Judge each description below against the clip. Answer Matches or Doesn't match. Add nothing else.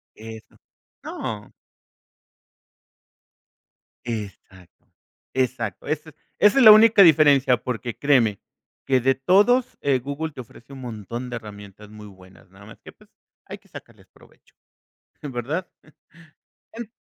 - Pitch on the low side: Matches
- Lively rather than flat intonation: Matches